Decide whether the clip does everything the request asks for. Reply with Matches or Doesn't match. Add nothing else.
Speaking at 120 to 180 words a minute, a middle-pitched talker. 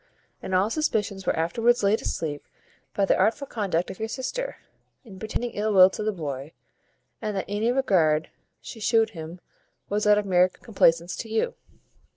Doesn't match